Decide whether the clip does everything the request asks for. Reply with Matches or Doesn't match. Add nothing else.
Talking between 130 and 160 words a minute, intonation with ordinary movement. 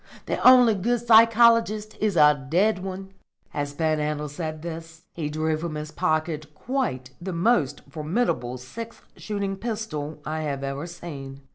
Doesn't match